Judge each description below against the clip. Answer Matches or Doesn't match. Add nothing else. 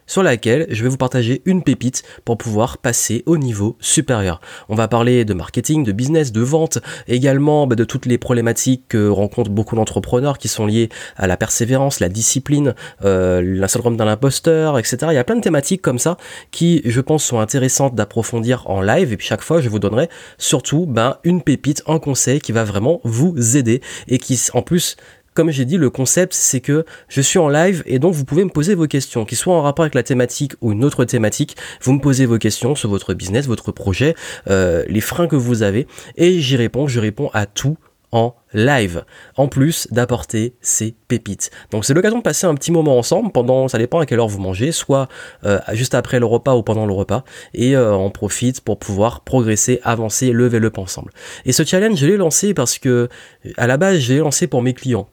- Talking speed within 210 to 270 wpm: Matches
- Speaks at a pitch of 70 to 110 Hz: Doesn't match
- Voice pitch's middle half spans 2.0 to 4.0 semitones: Doesn't match